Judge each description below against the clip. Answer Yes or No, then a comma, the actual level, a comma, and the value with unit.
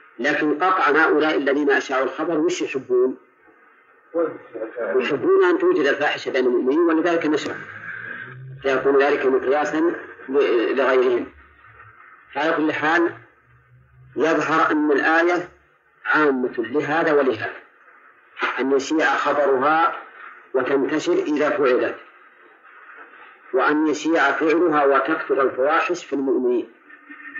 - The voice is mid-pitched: No, very high, 305 Hz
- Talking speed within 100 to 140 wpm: No, average, 90 wpm